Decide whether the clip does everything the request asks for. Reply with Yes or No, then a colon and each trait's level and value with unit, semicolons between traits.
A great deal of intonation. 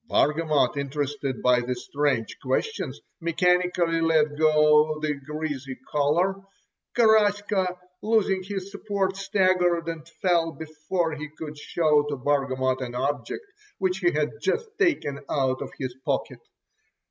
No: average, 4.4 semitones